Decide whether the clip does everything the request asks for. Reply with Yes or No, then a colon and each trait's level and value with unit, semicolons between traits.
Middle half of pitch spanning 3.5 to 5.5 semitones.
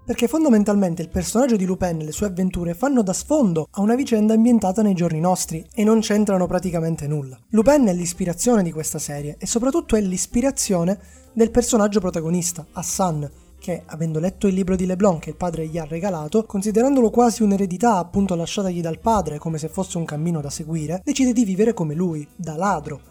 Yes: average, 4.9 semitones